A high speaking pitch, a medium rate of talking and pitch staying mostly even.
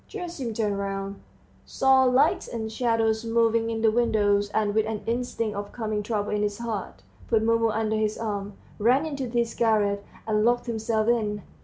Yes: high, 220 Hz; average, 175 wpm; narrow, 2.0 semitones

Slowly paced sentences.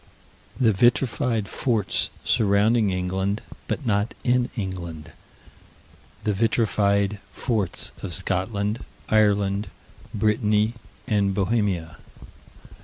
Yes: slow, 85 wpm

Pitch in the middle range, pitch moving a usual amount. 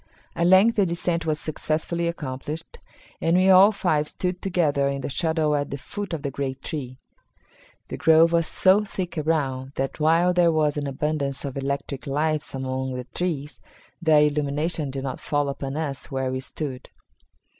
Yes: medium, 150 Hz; average, 3.5 semitones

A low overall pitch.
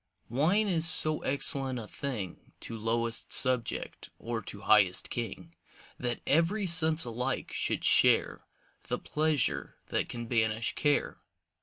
Yes: low, 125 Hz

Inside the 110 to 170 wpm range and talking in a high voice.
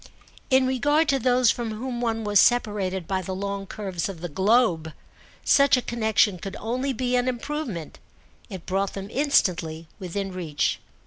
Yes: average, 165 wpm; high, 210 Hz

